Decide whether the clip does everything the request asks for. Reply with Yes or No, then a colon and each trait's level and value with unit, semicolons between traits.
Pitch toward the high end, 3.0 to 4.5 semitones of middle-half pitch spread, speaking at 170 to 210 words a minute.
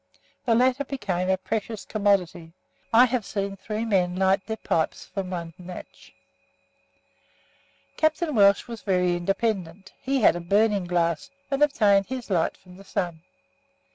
No: high, 195 Hz; average, 3.9 semitones; average, 145 wpm